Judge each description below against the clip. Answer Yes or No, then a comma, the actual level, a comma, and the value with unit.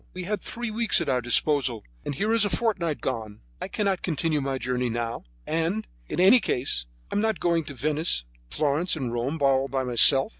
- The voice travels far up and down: Yes, wide, 6.5 semitones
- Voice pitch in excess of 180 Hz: No, medium, 150 Hz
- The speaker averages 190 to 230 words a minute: Yes, average, 200 wpm